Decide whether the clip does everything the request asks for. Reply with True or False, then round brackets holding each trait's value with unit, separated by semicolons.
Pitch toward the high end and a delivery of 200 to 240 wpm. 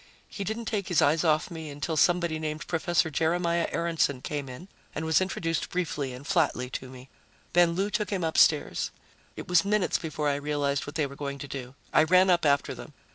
False (160 Hz; 205 wpm)